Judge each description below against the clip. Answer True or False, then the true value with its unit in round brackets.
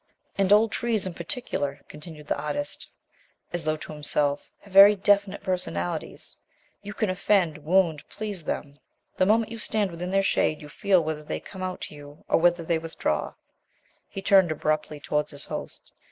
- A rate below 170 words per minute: False (175 wpm)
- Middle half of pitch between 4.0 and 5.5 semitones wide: True (4.8 semitones)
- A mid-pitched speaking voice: True (175 Hz)